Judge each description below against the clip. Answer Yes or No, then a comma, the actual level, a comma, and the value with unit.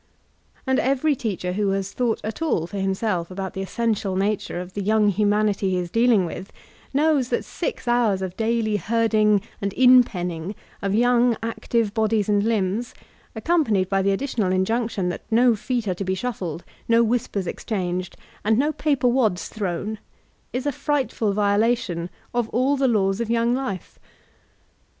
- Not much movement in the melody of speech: No, average, 3.8 semitones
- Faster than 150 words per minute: Yes, average, 170 wpm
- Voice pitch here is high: Yes, high, 215 Hz